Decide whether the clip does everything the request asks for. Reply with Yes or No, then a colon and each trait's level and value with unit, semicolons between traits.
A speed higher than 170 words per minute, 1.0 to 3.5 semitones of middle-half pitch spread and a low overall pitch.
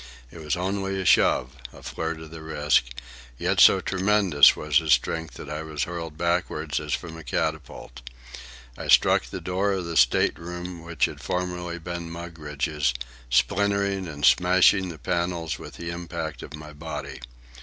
No: average, 165 wpm; average, 2.9 semitones; very low, 85 Hz